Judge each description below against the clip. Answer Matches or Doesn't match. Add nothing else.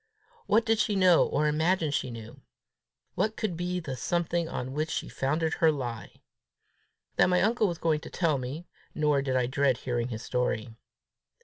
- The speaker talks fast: Doesn't match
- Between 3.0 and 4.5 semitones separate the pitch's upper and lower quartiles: Doesn't match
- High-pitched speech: Doesn't match